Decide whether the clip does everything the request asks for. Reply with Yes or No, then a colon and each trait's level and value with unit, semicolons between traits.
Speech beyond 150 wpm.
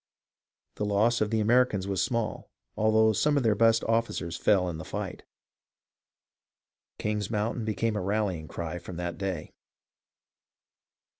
No: average, 145 wpm